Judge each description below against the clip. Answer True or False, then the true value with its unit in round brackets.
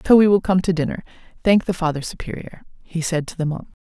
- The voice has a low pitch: False (175 Hz)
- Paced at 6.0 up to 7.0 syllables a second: True (6.5 syllables/s)